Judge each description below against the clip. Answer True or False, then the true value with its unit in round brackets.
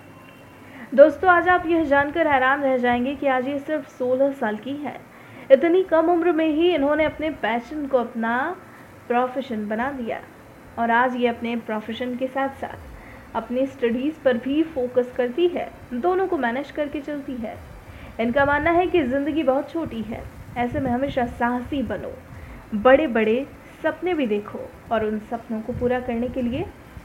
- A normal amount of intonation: True (3.8 semitones)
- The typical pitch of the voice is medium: False (265 Hz)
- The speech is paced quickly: False (170 wpm)